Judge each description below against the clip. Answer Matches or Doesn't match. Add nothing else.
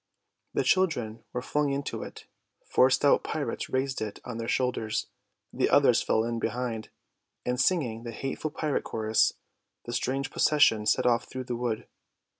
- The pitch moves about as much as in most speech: Matches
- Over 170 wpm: Doesn't match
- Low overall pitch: Matches